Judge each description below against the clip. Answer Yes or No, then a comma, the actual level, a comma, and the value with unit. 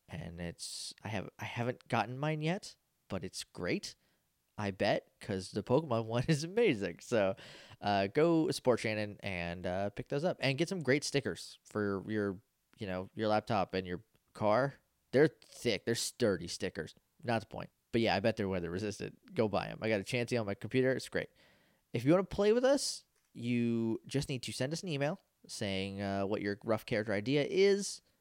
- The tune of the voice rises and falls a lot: Yes, wide, 5.9 semitones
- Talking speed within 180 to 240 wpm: Yes, average, 200 wpm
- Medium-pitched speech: No, low, 115 Hz